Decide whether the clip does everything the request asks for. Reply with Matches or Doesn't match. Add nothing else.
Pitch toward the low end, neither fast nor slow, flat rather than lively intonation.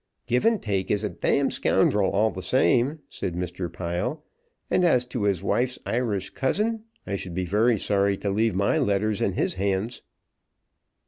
Doesn't match